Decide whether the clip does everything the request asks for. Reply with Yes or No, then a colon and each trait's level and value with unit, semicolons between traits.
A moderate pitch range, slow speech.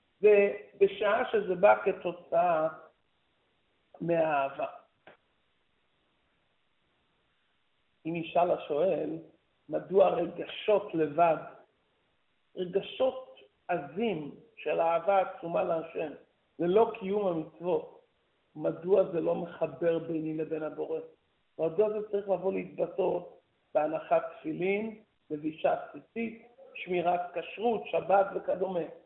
Yes: average, 4.7 semitones; slow, 85 wpm